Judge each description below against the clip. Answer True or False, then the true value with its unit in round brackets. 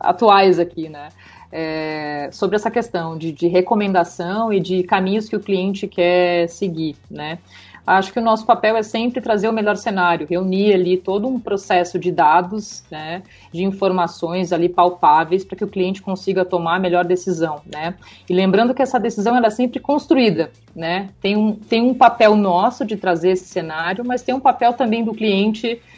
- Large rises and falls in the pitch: False (4.0 semitones)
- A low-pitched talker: False (190 Hz)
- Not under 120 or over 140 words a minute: False (180 wpm)